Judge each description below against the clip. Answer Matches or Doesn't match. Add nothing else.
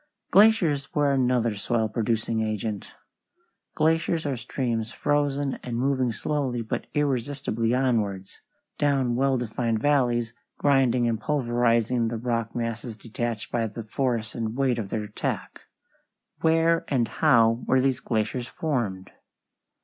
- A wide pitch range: Doesn't match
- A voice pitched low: Matches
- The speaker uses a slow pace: Matches